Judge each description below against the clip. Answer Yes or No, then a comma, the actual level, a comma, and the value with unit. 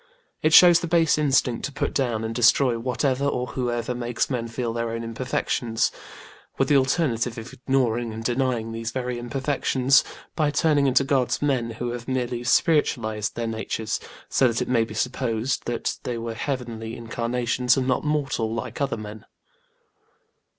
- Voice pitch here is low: Yes, low, 125 Hz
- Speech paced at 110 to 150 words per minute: No, average, 165 wpm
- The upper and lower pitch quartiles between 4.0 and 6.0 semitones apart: No, narrow, 2.6 semitones